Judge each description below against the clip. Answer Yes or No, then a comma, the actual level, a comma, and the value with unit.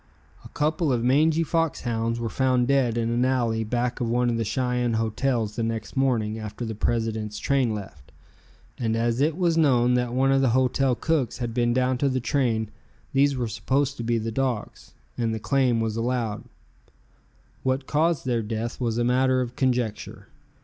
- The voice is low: Yes, low, 120 Hz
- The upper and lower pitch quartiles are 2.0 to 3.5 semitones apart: Yes, narrow, 2.6 semitones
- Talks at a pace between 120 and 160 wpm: No, average, 190 wpm